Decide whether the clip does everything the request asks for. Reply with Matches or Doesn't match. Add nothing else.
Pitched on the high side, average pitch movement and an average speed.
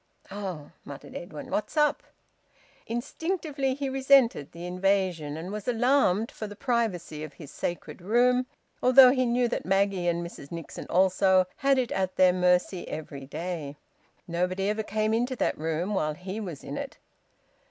Doesn't match